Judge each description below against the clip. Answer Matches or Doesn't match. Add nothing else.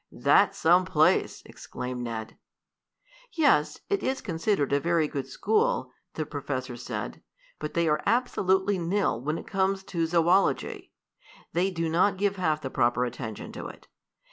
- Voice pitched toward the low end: Doesn't match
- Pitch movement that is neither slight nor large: Matches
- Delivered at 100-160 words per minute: Matches